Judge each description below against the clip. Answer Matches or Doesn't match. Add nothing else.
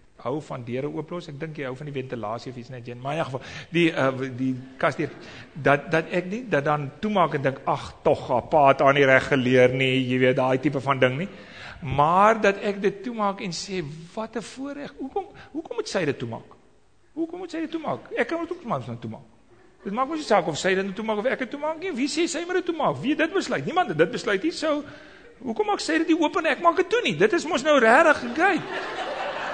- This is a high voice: Matches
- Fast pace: Matches